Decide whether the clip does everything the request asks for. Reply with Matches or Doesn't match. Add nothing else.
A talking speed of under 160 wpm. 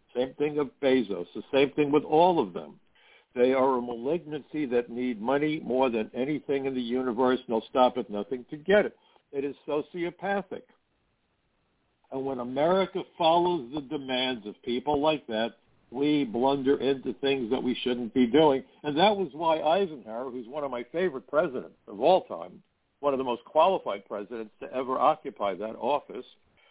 Doesn't match